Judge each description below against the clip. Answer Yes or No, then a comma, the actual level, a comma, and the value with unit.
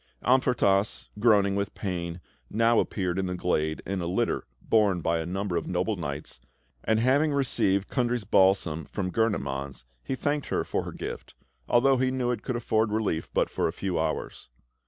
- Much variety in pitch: No, average, 5.0 semitones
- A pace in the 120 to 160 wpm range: No, average, 175 wpm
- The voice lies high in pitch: No, low, 100 Hz